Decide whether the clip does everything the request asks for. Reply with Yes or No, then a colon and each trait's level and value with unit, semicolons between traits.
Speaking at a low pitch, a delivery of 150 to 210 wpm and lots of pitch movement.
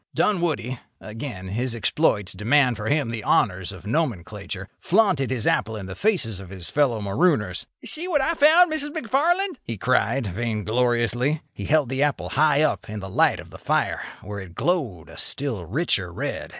Yes: low, 120 Hz; average, 170 wpm; wide, 7.6 semitones